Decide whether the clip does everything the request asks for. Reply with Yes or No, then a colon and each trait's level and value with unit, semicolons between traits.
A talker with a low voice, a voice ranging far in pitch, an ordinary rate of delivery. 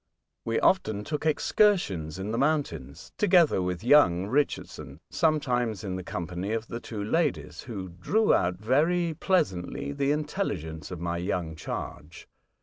Yes: low, 110 Hz; wide, 9.0 semitones; average, 145 wpm